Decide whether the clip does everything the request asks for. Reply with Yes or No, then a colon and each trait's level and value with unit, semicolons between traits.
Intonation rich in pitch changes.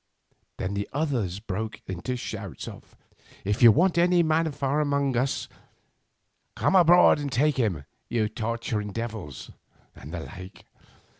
Yes: wide, 6.3 semitones